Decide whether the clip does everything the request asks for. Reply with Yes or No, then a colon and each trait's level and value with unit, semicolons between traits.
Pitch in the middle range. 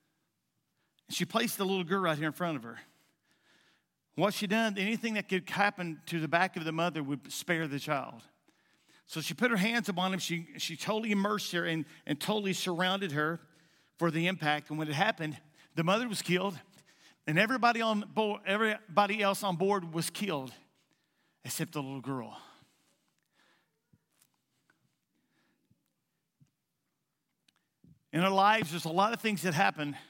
Yes: medium, 180 Hz